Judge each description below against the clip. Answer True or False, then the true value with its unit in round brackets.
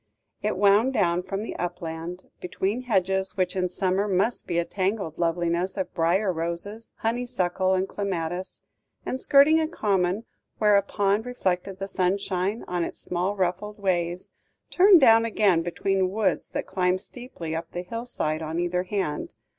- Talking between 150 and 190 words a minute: True (160 wpm)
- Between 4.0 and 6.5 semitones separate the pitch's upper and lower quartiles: False (2.9 semitones)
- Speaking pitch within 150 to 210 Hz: True (190 Hz)